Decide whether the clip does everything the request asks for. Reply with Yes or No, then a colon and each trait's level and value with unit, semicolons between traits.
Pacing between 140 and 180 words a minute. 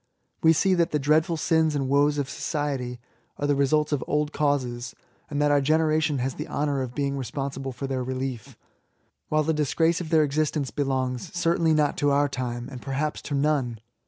No: average, 190 wpm